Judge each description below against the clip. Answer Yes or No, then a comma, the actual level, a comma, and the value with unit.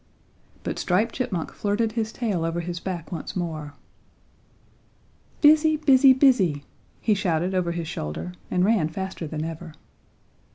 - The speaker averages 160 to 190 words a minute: No, slow, 135 wpm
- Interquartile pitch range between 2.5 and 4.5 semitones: No, wide, 5.5 semitones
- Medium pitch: Yes, medium, 180 Hz